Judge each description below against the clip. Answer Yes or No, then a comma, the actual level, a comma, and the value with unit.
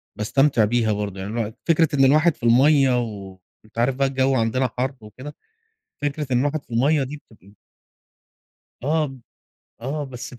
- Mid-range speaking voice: No, low, 130 Hz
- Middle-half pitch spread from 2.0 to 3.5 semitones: No, average, 4.1 semitones